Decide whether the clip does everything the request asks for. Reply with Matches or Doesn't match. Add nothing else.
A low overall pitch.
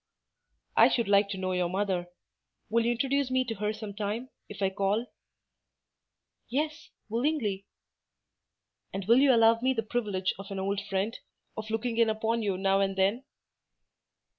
Doesn't match